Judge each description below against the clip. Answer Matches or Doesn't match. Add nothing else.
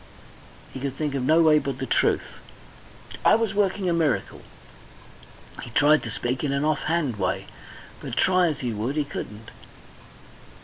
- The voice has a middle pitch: Matches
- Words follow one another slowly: Doesn't match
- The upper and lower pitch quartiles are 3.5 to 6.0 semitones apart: Matches